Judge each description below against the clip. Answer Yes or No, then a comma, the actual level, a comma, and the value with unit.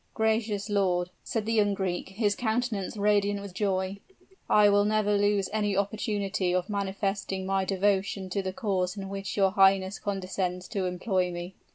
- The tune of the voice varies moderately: No, narrow, 1.5 semitones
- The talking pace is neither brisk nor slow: Yes, average, 165 wpm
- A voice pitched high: Yes, high, 200 Hz